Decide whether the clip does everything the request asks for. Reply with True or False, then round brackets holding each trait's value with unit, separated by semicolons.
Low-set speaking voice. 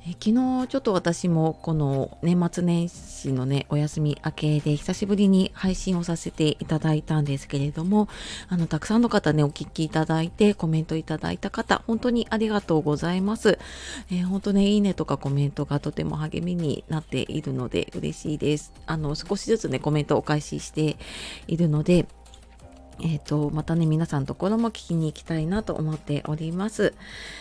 False (160 Hz)